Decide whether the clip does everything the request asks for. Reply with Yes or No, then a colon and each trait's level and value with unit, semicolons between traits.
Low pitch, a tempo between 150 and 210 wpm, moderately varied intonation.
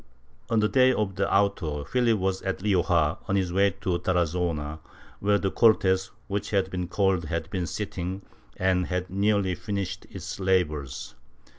No: very low, 95 Hz; average, 165 wpm; narrow, 2.3 semitones